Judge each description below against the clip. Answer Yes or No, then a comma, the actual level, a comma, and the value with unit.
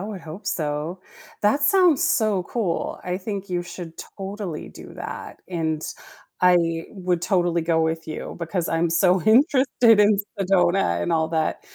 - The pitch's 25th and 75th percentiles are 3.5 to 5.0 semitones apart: Yes, average, 4.0 semitones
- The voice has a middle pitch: Yes, medium, 180 Hz